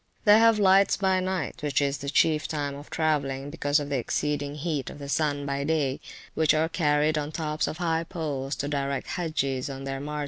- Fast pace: Yes, fast, 220 wpm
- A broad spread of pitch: No, narrow, 2.4 semitones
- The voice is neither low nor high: Yes, medium, 150 Hz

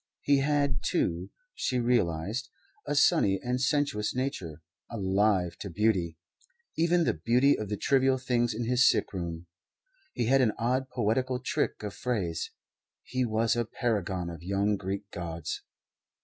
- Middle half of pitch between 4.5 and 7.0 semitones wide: Yes, average, 5.2 semitones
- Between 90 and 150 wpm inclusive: Yes, average, 145 wpm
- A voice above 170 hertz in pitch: No, low, 115 Hz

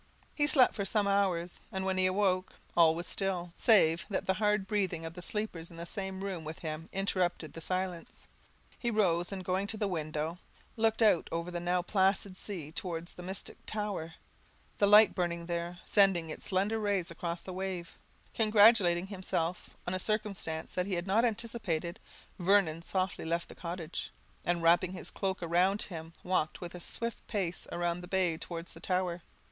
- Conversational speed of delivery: Yes, average, 180 wpm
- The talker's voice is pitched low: No, medium, 185 Hz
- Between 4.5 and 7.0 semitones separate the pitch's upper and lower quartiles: No, average, 2.8 semitones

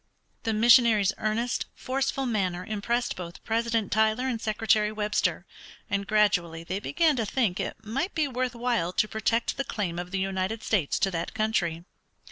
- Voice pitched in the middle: No, high, 215 Hz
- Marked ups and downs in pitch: No, average, 3.5 semitones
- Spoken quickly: No, average, 165 wpm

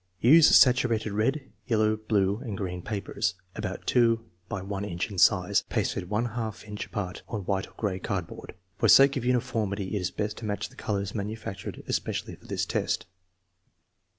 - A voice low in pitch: Yes, low, 105 Hz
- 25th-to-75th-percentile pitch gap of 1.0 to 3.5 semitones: Yes, average, 2.8 semitones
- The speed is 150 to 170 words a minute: Yes, average, 165 wpm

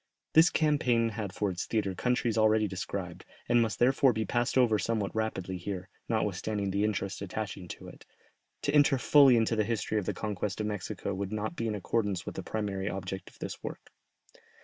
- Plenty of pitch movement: No, average, 3.0 semitones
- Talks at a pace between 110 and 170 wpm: No, average, 195 wpm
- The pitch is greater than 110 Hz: No, low, 105 Hz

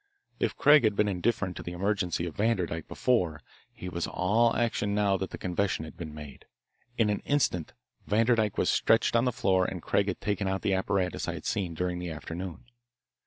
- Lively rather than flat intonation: No, average, 3.3 semitones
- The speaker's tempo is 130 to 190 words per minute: No, average, 200 wpm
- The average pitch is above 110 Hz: No, very low, 95 Hz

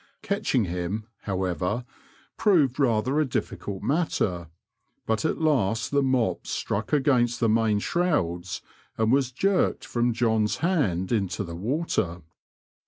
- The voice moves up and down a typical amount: No, wide, 6.6 semitones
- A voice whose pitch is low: Yes, low, 115 Hz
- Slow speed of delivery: Yes, slow, 125 wpm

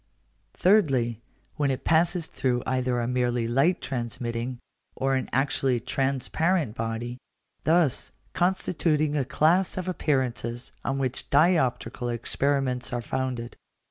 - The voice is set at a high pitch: No, low, 130 Hz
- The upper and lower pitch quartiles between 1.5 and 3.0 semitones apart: No, average, 4.1 semitones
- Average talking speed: No, slow, 115 wpm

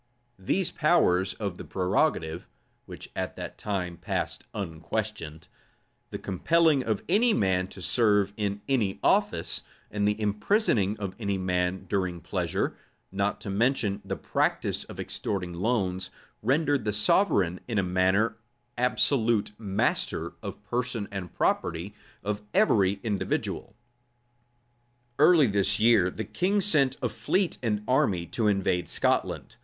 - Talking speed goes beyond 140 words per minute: No, slow, 135 wpm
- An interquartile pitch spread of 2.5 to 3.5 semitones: No, average, 4.5 semitones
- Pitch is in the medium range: No, low, 105 Hz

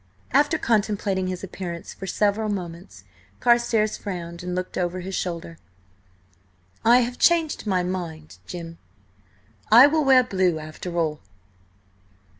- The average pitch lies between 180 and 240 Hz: Yes, medium, 185 Hz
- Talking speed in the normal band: No, slow, 125 wpm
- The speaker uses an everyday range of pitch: Yes, average, 4.7 semitones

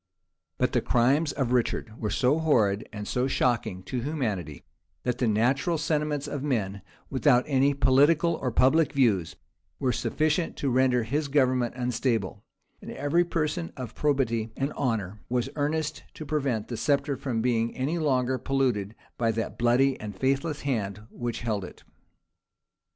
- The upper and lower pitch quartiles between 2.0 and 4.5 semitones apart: Yes, average, 4.0 semitones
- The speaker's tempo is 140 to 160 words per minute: Yes, average, 155 wpm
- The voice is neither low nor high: No, low, 130 Hz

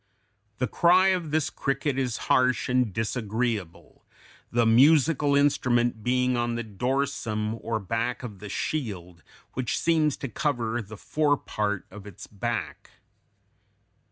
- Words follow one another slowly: Yes, slow, 130 wpm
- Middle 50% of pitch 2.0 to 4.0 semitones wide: No, average, 4.5 semitones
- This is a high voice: No, low, 120 Hz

